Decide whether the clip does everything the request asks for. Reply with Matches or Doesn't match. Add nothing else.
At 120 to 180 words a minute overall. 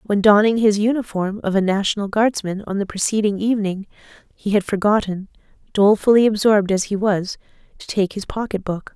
Matches